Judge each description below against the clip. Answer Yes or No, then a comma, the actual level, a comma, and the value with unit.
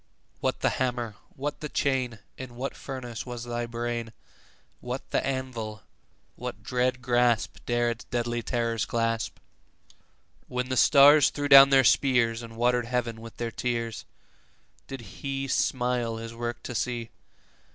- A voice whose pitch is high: No, low, 120 Hz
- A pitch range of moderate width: No, narrow, 1.9 semitones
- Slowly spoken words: No, average, 150 wpm